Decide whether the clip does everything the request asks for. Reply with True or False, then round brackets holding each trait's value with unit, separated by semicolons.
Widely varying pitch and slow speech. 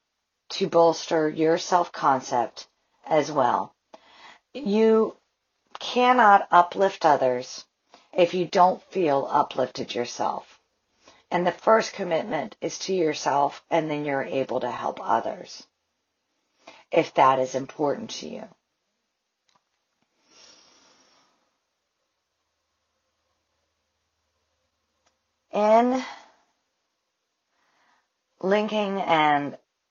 True (7.2 semitones; 80 wpm)